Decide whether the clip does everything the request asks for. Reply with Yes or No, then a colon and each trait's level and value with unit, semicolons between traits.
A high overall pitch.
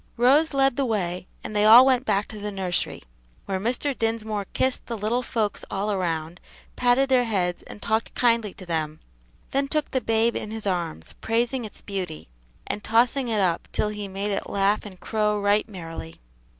Yes: high, 210 Hz